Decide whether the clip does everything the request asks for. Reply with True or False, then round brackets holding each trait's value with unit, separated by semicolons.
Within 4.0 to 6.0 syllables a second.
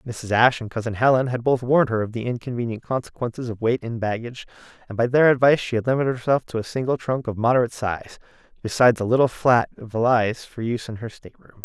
False (6.8 syllables/s)